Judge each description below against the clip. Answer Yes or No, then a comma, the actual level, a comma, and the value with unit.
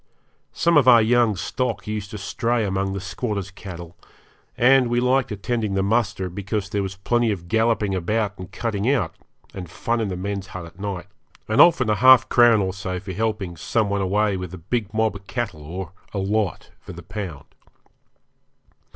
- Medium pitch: No, low, 100 Hz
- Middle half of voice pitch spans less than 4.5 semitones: Yes, average, 3.3 semitones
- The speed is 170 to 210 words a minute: Yes, average, 190 wpm